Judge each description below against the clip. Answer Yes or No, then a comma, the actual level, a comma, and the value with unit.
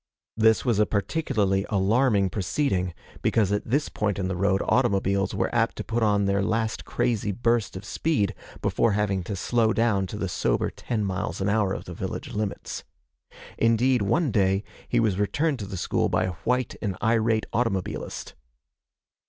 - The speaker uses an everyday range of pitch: Yes, average, 3.0 semitones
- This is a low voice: Yes, low, 105 Hz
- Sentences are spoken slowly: No, average, 175 wpm